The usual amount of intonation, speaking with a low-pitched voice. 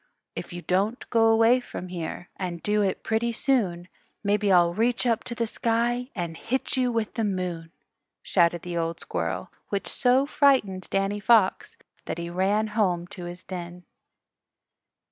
No: average, 4.7 semitones; high, 200 Hz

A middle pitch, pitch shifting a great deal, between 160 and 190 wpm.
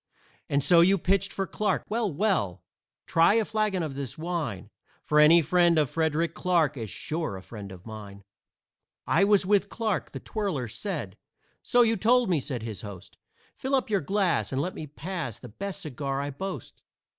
Yes: medium, 165 Hz; wide, 6.7 semitones; average, 185 wpm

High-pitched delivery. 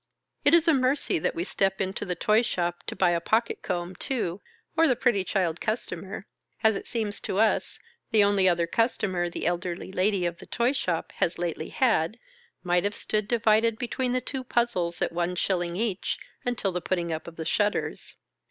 Yes: high, 195 Hz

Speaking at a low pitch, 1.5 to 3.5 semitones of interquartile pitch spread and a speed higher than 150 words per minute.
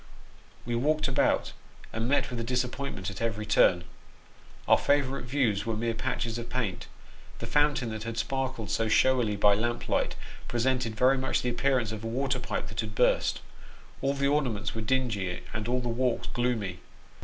Yes: low, 120 Hz; average, 3.1 semitones; average, 180 wpm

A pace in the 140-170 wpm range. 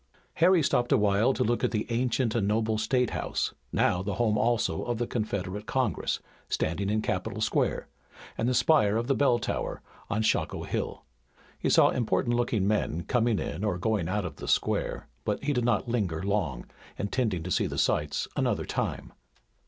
No: average, 185 wpm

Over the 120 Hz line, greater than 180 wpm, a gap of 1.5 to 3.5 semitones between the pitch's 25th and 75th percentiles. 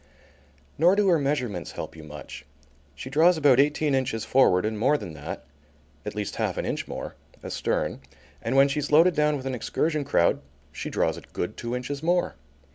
No: low, 135 Hz; average, 190 wpm; wide, 5.4 semitones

